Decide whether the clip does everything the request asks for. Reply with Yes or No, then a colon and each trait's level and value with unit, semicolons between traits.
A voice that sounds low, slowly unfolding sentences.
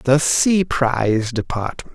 Yes: low, 130 Hz; slow, 125 wpm